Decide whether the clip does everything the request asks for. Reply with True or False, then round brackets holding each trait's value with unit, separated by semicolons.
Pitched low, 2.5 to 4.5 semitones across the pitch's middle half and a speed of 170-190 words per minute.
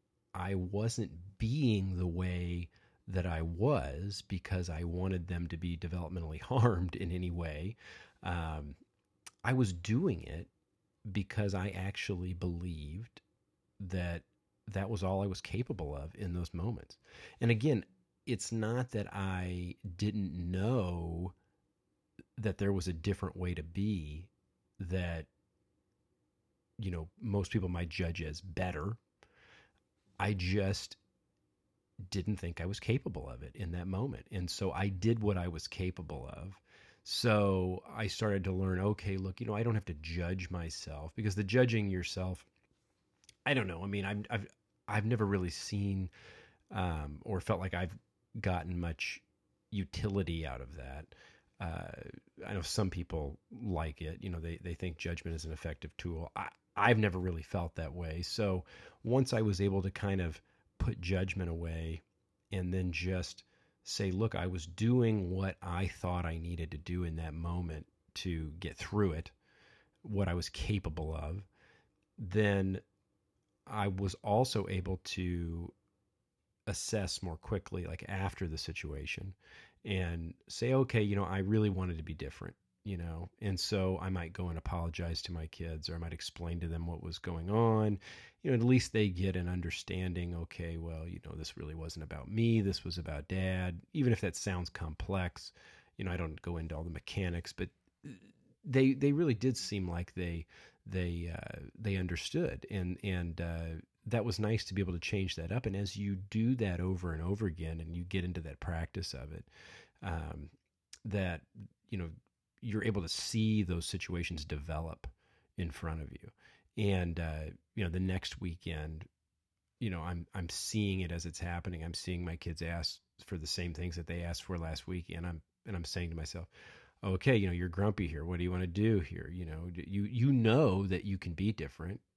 True (90 Hz; 3.1 semitones; 175 wpm)